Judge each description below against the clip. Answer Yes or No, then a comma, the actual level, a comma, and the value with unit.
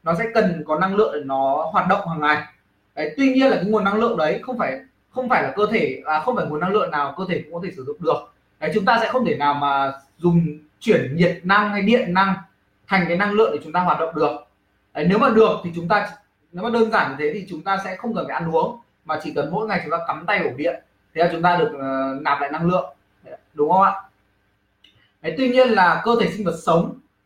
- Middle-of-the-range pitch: Yes, medium, 175 Hz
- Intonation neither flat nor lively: No, wide, 6.0 semitones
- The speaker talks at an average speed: No, fast, 270 wpm